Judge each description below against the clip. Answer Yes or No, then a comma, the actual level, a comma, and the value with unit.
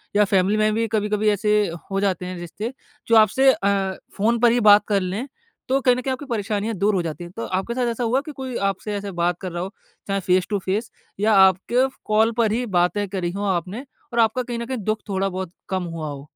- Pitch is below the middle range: No, high, 205 Hz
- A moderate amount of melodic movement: Yes, average, 3.4 semitones